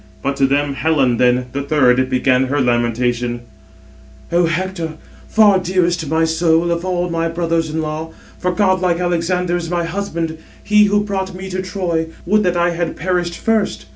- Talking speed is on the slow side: No, average, 170 wpm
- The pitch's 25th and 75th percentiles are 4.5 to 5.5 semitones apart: No, average, 3.8 semitones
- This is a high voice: No, medium, 170 Hz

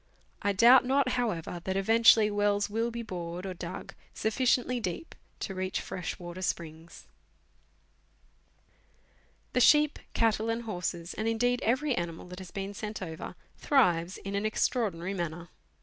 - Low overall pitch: No, high, 205 Hz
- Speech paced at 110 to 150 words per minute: Yes, average, 145 wpm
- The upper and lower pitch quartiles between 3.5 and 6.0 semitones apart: Yes, average, 4.7 semitones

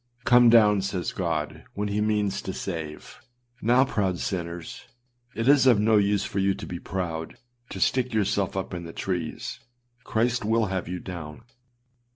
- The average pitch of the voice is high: No, low, 100 Hz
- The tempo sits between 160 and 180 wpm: Yes, average, 170 wpm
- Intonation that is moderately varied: Yes, average, 3.7 semitones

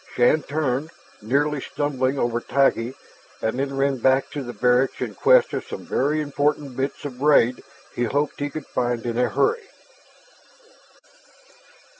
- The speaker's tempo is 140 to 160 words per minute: Yes, average, 150 wpm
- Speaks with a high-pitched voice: No, low, 135 Hz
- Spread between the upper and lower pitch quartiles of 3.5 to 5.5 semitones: No, average, 2.9 semitones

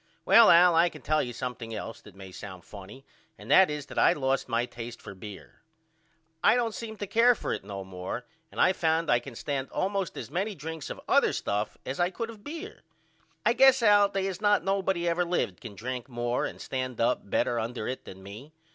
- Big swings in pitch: Yes, wide, 8.9 semitones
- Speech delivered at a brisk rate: Yes, fast, 220 wpm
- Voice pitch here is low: No, medium, 145 Hz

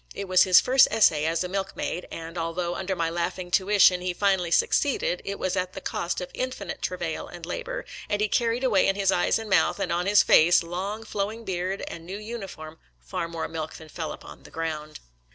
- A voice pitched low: No, medium, 185 Hz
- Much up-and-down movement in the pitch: No, average, 3.4 semitones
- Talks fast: Yes, fast, 220 wpm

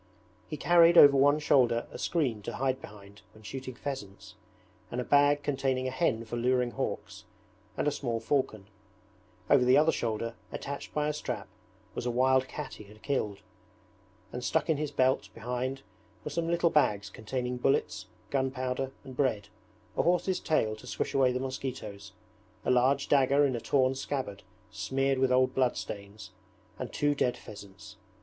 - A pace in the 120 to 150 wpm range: No, average, 170 wpm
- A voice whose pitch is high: No, low, 130 Hz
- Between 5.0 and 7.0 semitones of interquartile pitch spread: No, average, 3.3 semitones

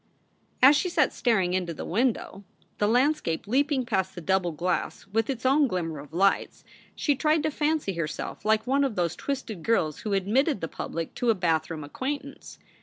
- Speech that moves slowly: No, average, 180 wpm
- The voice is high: Yes, high, 215 Hz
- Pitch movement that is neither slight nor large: No, wide, 7.5 semitones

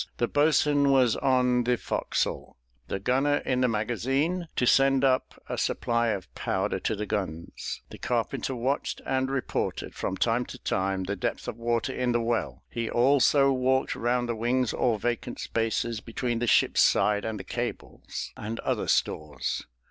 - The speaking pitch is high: No, low, 120 Hz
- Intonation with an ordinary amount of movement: Yes, average, 3.1 semitones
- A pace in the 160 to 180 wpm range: Yes, average, 170 wpm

